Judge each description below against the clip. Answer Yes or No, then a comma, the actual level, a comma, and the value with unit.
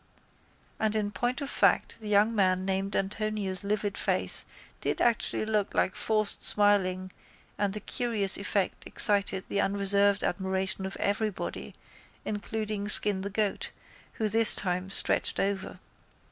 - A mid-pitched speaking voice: No, high, 205 Hz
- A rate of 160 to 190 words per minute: No, slow, 135 wpm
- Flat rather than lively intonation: Yes, narrow, 1.8 semitones